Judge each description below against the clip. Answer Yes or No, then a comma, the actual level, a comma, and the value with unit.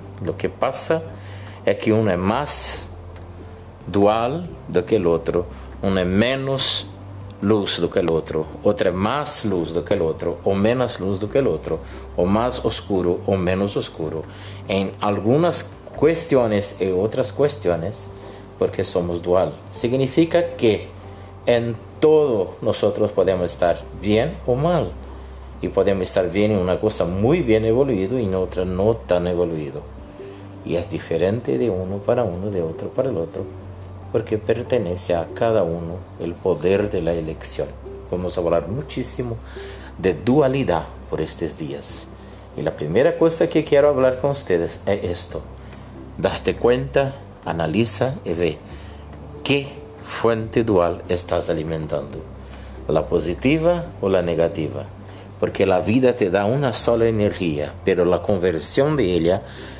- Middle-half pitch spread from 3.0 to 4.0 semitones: No, average, 4.7 semitones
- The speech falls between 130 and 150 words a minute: Yes, average, 145 wpm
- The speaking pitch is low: Yes, low, 100 Hz